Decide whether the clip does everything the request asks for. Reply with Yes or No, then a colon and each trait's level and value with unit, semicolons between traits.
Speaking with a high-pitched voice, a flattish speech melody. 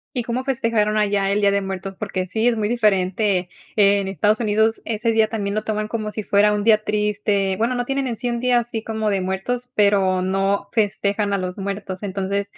Yes: high, 210 Hz; narrow, 2.1 semitones